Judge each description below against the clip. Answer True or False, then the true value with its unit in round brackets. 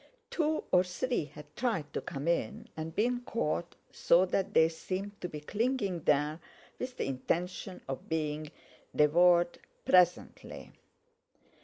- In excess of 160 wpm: False (135 wpm)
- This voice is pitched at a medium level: True (175 Hz)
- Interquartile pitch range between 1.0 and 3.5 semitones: False (5.0 semitones)